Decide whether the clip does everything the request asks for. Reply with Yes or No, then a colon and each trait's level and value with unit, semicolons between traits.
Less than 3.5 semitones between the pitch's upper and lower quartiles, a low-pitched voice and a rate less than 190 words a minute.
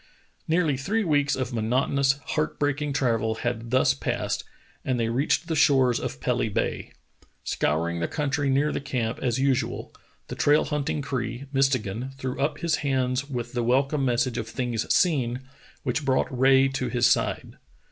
Yes: average, 2.9 semitones; low, 130 Hz; average, 165 wpm